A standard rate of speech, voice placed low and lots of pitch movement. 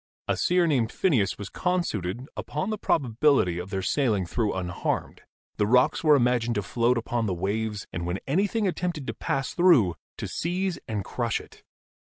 Yes: average, 195 wpm; low, 120 Hz; wide, 7.7 semitones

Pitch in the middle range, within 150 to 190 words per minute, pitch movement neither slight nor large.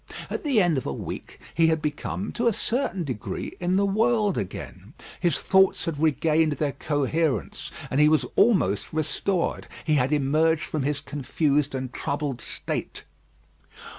Yes: medium, 155 Hz; average, 160 wpm; average, 4.3 semitones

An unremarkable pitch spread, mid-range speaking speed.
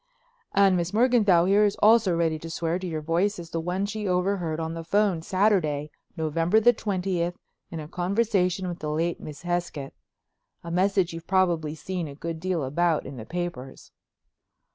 Yes: average, 3.1 semitones; average, 175 wpm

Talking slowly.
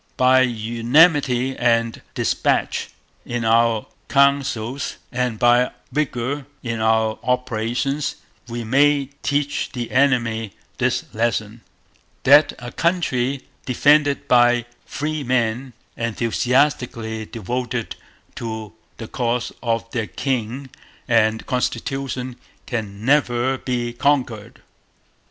Yes: slow, 95 wpm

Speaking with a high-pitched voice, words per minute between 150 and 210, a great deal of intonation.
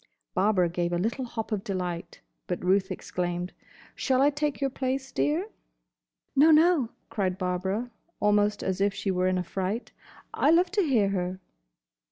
Yes: high, 205 Hz; average, 165 wpm; wide, 6.5 semitones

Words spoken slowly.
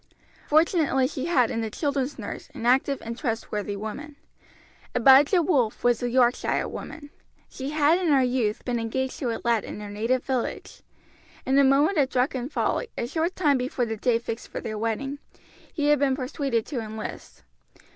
No: average, 180 wpm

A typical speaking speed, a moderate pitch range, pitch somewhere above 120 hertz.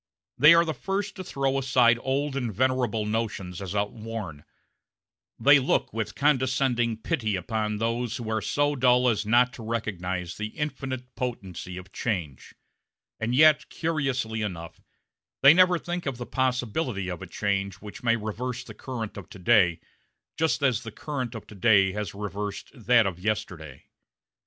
No: average, 160 wpm; average, 4.2 semitones; low, 115 Hz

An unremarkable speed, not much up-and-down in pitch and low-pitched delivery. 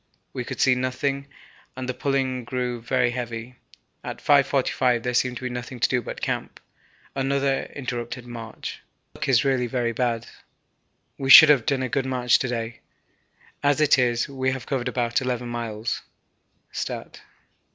Yes: average, 160 wpm; narrow, 1.8 semitones; low, 125 Hz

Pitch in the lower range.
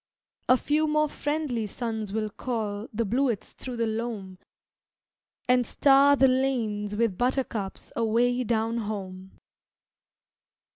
No: high, 230 Hz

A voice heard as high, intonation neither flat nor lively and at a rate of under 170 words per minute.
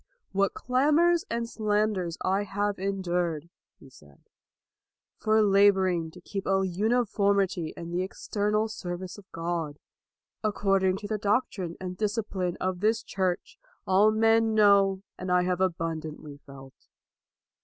Yes: high, 195 Hz; average, 3.1 semitones; average, 140 wpm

